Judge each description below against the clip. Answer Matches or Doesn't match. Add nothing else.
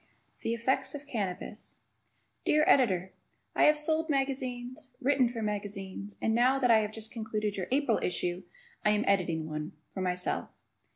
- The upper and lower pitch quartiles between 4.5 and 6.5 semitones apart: Matches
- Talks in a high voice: Matches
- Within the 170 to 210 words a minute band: Doesn't match